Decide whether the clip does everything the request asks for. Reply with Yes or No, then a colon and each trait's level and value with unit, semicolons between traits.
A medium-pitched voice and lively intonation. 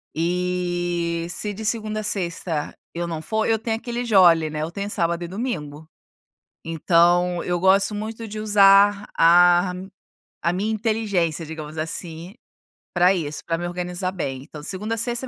No: medium, 180 Hz; average, 3.8 semitones